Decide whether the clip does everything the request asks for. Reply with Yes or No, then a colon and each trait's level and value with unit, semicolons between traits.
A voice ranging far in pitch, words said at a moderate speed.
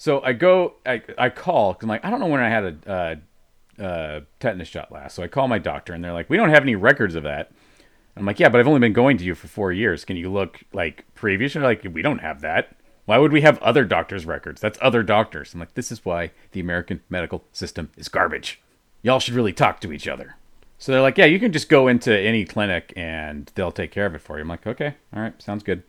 No: wide, 6.4 semitones; fast, 265 wpm